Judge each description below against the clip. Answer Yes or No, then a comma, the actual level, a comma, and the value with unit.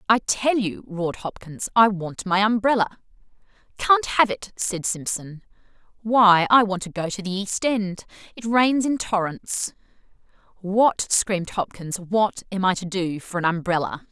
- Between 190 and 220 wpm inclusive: No, average, 155 wpm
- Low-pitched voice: No, high, 200 Hz